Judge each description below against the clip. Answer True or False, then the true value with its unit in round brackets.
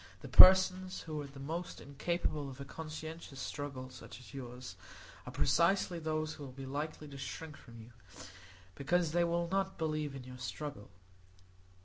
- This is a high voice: False (150 Hz)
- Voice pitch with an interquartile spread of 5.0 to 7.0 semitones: False (3.7 semitones)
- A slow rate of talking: False (165 wpm)